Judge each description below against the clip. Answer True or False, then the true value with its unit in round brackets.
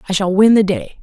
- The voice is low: False (200 Hz)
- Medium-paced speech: False (295 wpm)